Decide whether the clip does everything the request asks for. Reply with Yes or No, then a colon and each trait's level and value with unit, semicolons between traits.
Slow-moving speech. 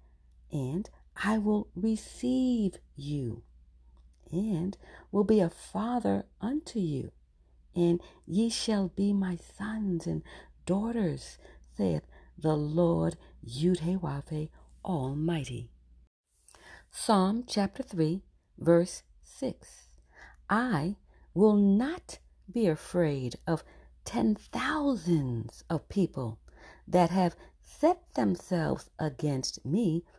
Yes: slow, 90 wpm